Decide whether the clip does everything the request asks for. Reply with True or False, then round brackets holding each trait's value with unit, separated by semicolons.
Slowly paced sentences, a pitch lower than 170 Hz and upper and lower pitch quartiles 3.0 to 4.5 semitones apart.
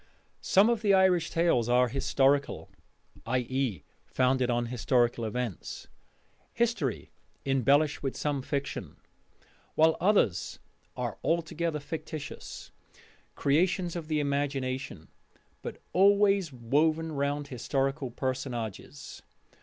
True (100 wpm; 140 Hz; 4.2 semitones)